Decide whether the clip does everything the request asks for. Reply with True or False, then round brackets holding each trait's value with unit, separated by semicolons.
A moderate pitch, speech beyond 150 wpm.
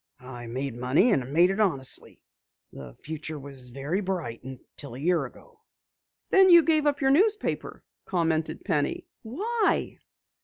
False (160 Hz; 145 wpm)